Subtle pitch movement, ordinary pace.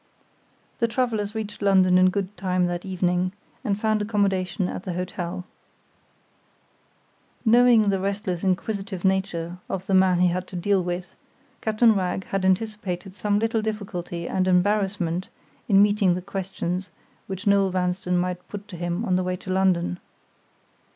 Yes: narrow, 2.2 semitones; average, 150 wpm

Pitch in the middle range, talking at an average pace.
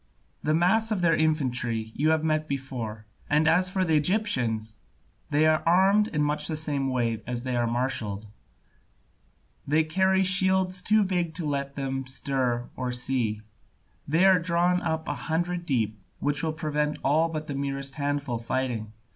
Yes: medium, 150 Hz; average, 165 wpm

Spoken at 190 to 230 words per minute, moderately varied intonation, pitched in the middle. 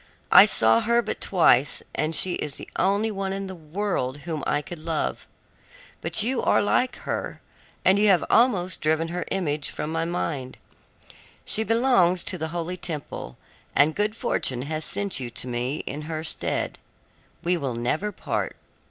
No: average, 170 wpm; average, 4.8 semitones; medium, 170 Hz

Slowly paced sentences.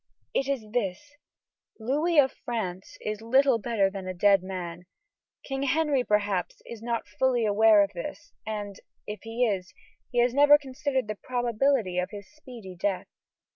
No: average, 160 wpm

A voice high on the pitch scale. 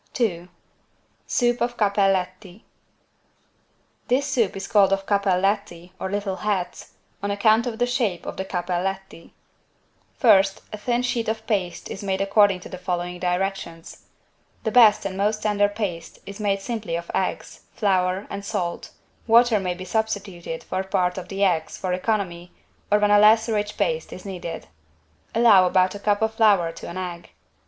Yes: high, 195 Hz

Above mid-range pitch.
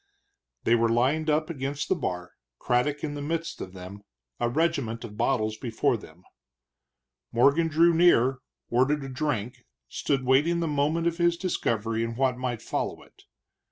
No: low, 135 Hz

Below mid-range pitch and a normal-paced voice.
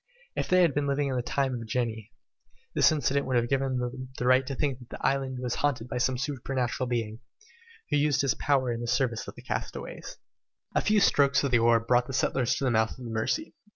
No: low, 130 Hz; fast, 235 wpm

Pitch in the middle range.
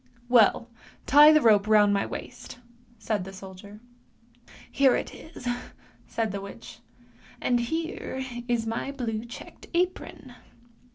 No: high, 235 Hz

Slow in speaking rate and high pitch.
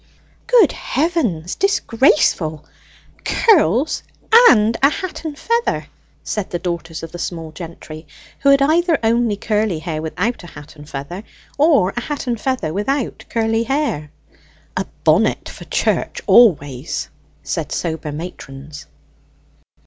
Yes: slow, 130 wpm; high, 210 Hz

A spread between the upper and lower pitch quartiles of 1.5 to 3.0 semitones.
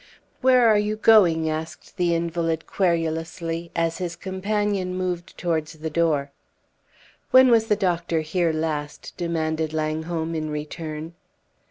Yes: average, 2.7 semitones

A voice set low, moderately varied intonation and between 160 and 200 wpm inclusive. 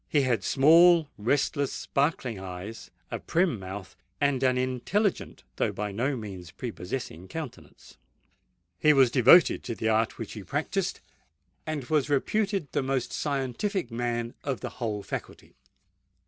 No: low, 130 Hz; average, 4.8 semitones; average, 140 wpm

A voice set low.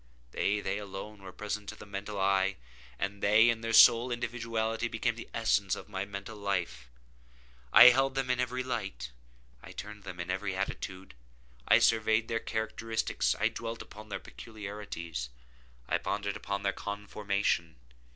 Yes: low, 105 Hz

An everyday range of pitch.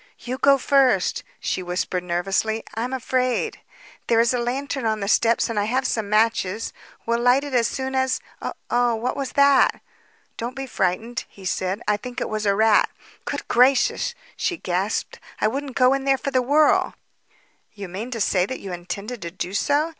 Yes: average, 4.3 semitones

